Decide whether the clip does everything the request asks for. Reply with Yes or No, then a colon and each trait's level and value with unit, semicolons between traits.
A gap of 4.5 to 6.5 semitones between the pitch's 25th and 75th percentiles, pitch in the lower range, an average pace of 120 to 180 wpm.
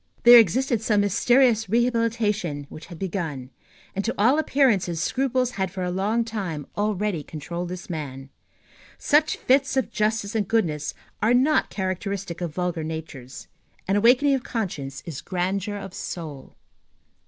No: wide, 5.4 semitones; high, 200 Hz; average, 150 wpm